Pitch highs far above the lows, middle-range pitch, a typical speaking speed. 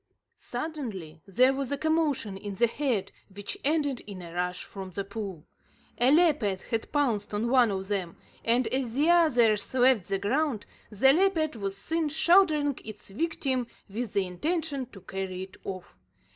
No: wide, 6.7 semitones; high, 235 Hz; average, 165 wpm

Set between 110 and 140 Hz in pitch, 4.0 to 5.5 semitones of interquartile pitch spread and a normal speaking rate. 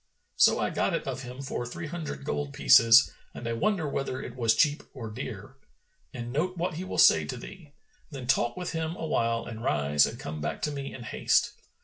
No: low, 135 Hz; average, 4.7 semitones; fast, 215 wpm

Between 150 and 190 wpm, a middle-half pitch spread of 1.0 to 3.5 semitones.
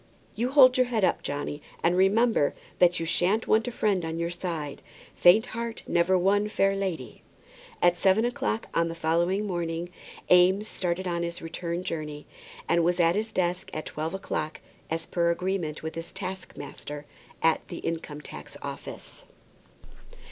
Yes: average, 160 wpm; average, 2.9 semitones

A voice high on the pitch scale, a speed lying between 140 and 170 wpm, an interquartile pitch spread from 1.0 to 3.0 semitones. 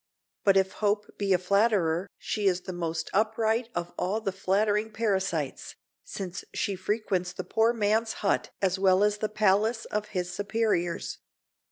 Yes: high, 200 Hz; average, 160 wpm; average, 2.7 semitones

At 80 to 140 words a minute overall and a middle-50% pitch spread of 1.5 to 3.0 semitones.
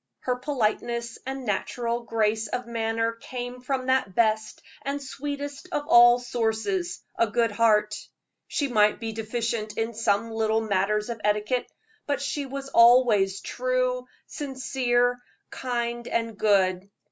Yes: slow, 135 wpm; average, 2.7 semitones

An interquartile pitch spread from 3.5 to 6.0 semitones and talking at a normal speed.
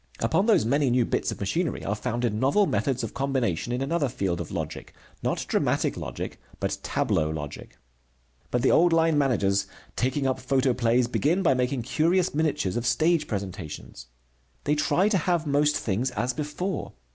Yes: average, 5.1 semitones; average, 170 wpm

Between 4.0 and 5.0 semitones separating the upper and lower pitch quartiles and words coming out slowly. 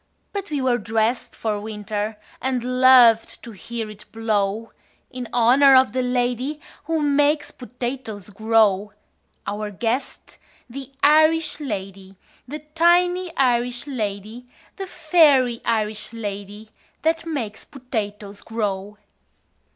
Yes: average, 4.6 semitones; slow, 115 wpm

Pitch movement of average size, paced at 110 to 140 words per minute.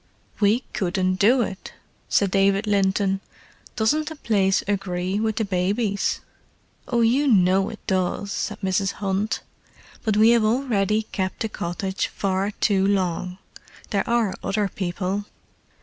No: narrow, 2.3 semitones; slow, 135 wpm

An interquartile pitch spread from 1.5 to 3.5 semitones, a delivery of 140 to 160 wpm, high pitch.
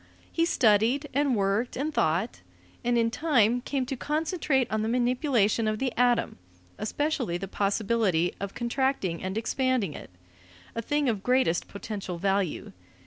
No: average, 4.8 semitones; average, 145 wpm; high, 235 Hz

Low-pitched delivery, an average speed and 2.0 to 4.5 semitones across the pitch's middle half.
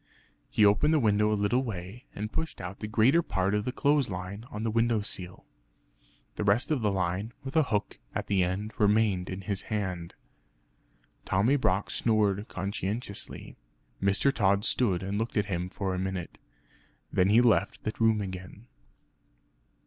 Yes: low, 105 Hz; average, 170 wpm; average, 2.9 semitones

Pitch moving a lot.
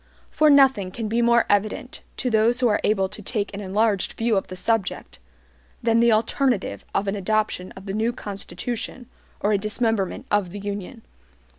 No: average, 2.8 semitones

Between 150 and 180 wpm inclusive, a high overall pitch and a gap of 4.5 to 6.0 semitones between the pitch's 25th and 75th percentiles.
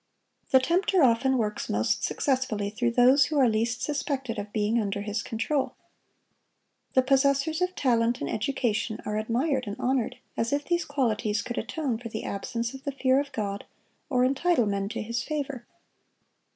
No: average, 170 wpm; high, 245 Hz; average, 4.1 semitones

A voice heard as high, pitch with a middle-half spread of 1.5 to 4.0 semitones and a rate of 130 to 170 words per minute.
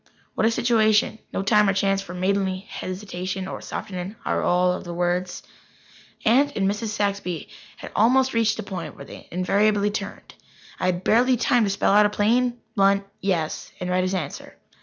No: high, 200 Hz; average, 2.9 semitones; average, 180 wpm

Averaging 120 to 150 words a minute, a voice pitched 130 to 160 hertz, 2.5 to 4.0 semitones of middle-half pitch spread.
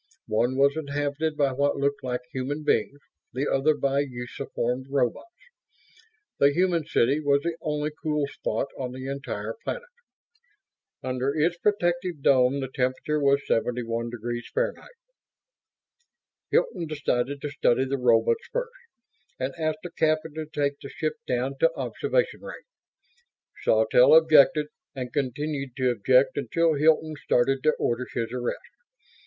Yes: slow, 135 wpm; medium, 140 Hz; average, 3.4 semitones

